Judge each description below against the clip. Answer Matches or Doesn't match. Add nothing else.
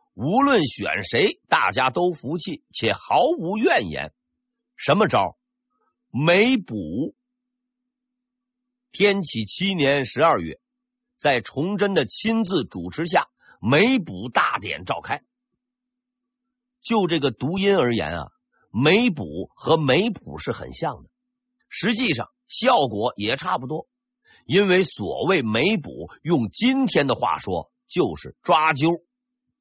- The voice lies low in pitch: Doesn't match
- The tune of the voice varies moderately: Doesn't match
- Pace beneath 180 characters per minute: Matches